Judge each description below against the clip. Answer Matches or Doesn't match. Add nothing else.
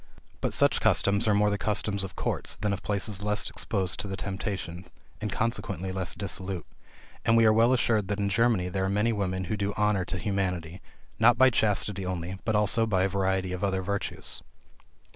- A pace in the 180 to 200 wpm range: Matches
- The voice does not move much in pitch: Matches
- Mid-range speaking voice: Doesn't match